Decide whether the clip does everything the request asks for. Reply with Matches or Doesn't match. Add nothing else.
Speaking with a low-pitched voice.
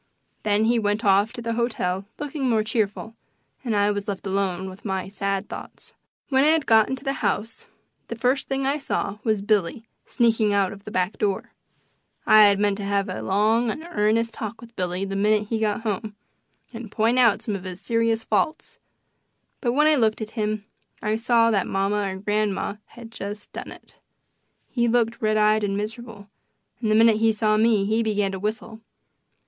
Doesn't match